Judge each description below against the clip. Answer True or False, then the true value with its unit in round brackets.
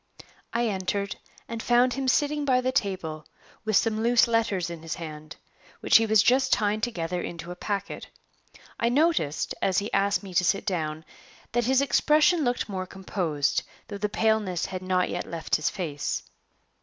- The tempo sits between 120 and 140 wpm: False (175 wpm)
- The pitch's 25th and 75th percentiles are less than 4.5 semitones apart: False (5.2 semitones)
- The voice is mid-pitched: False (200 Hz)